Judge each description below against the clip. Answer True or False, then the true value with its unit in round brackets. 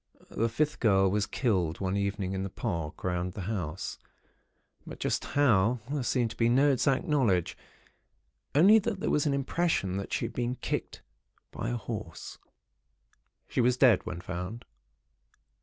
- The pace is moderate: True (160 wpm)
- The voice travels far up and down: True (6.2 semitones)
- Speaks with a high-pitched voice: False (115 Hz)